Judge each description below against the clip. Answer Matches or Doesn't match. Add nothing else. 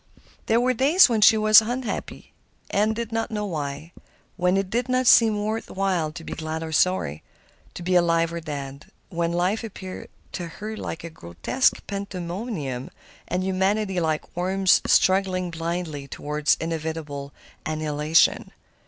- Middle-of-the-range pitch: Matches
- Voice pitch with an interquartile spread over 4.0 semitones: Matches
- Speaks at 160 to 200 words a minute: Doesn't match